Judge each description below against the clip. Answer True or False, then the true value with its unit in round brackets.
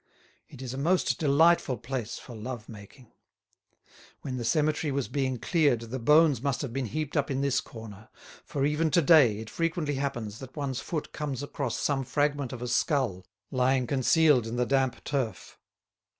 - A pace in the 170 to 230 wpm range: True (180 wpm)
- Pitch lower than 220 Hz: True (135 Hz)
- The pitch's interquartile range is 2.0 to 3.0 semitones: False (3.4 semitones)